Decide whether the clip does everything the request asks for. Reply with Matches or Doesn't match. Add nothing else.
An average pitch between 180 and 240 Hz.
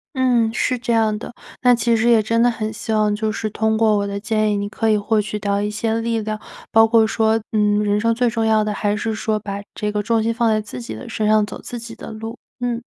Matches